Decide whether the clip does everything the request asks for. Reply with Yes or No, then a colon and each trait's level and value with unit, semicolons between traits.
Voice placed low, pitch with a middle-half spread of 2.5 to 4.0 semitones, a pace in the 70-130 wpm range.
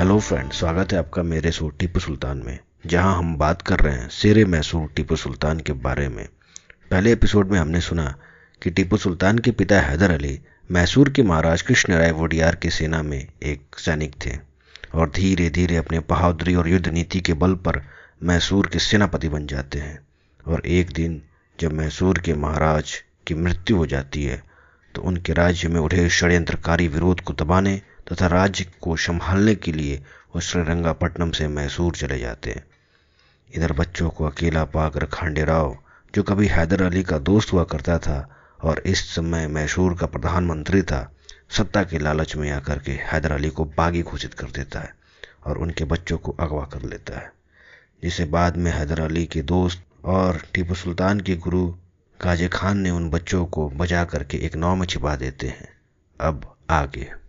No: very low, 85 Hz; average, 2.8 semitones; average, 180 wpm